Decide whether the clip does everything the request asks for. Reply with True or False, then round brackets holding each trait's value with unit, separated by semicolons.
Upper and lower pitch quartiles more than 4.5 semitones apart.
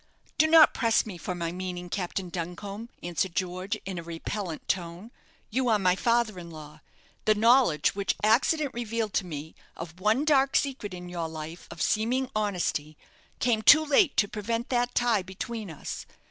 True (5.1 semitones)